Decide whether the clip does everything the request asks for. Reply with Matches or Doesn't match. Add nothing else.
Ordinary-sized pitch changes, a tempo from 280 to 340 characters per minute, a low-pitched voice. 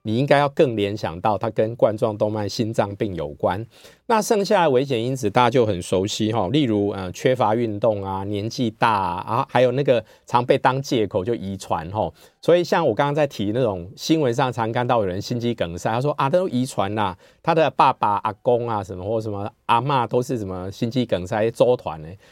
Matches